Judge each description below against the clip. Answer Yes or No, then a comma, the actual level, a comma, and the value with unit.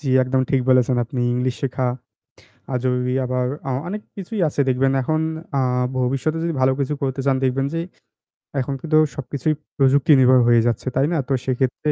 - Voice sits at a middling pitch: No, low, 130 Hz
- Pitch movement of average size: No, narrow, 2.1 semitones